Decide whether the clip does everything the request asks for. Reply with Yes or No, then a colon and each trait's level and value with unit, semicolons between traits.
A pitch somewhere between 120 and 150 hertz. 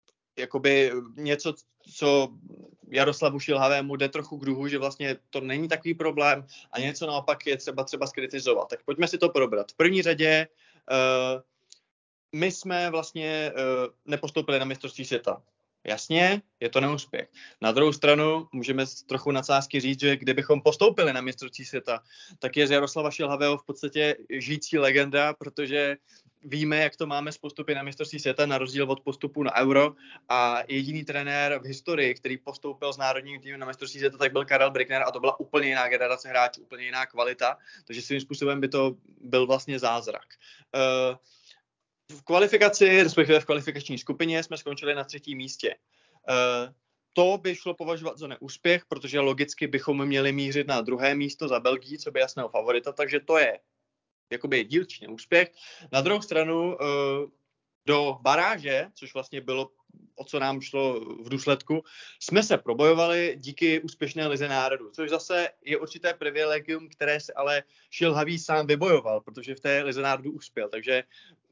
Yes: medium, 140 Hz